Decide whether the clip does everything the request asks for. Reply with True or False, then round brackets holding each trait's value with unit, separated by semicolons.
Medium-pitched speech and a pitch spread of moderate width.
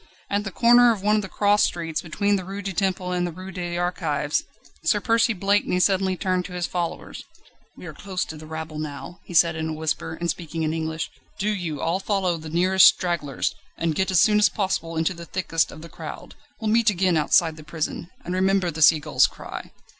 True (175 Hz; 3.3 semitones)